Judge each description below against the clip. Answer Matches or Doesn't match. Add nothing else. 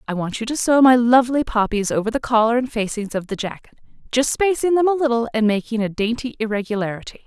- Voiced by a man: Doesn't match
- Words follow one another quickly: Matches